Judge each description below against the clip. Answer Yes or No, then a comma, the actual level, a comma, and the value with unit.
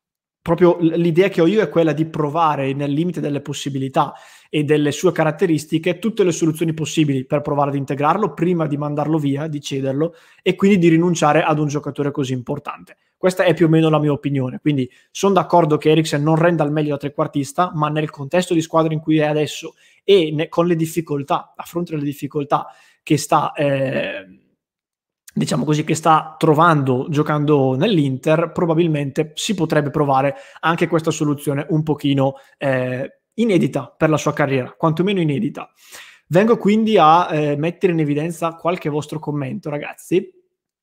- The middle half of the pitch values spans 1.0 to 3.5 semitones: Yes, narrow, 2.6 semitones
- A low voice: No, medium, 155 Hz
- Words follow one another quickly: No, average, 170 wpm